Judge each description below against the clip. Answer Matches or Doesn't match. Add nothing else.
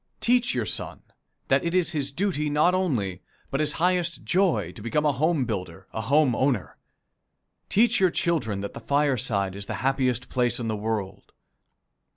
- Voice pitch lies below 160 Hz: Matches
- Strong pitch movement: Matches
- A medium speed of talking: Matches